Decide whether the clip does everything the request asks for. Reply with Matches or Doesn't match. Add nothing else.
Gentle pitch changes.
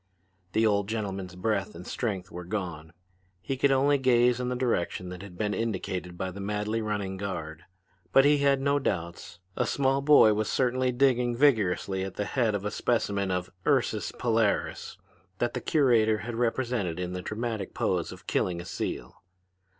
Doesn't match